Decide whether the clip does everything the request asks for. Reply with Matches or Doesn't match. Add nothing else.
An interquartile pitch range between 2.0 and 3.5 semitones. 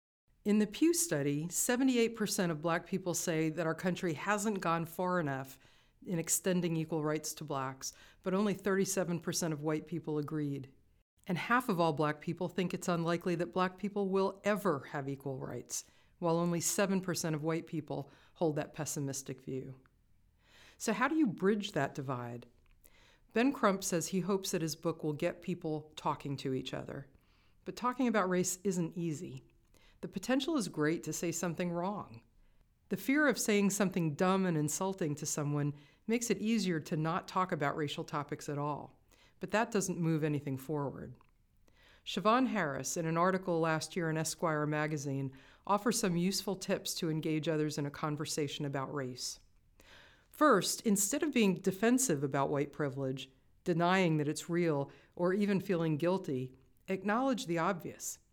Doesn't match